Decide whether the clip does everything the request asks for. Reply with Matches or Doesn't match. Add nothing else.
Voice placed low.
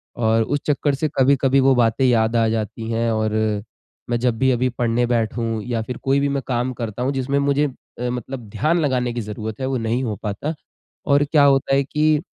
Matches